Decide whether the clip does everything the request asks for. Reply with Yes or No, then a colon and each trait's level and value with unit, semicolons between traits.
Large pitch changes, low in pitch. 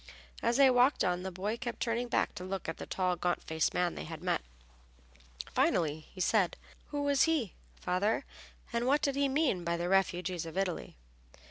No: wide, 5.8 semitones; high, 190 Hz